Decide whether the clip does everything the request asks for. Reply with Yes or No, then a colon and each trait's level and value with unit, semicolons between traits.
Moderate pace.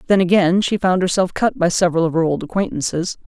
No: fast, 215 wpm